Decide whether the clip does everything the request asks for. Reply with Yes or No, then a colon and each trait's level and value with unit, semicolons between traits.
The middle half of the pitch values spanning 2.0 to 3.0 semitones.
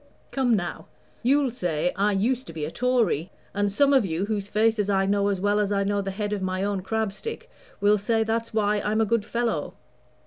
Yes: narrow, 2.4 semitones